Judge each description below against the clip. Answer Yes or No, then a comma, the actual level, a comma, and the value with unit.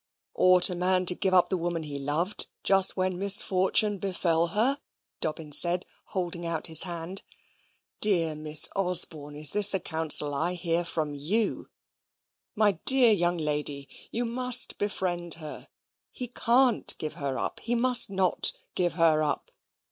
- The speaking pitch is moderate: Yes, medium, 175 Hz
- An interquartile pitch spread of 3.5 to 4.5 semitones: Yes, average, 3.8 semitones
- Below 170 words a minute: Yes, average, 155 wpm